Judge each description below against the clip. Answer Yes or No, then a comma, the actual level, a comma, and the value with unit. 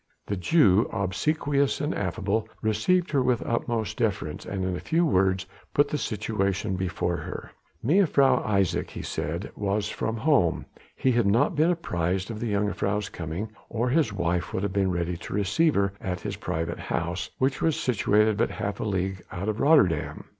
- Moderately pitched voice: No, low, 105 Hz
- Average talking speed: Yes, average, 175 wpm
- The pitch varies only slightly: No, average, 5.2 semitones